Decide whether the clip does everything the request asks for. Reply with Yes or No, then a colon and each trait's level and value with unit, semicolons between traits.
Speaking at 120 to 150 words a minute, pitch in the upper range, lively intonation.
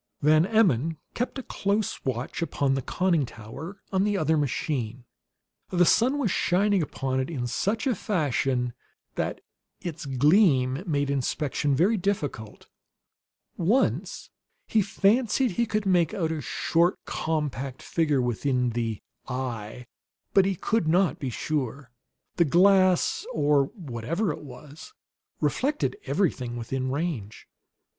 No: slow, 135 wpm; medium, 155 Hz; wide, 6.7 semitones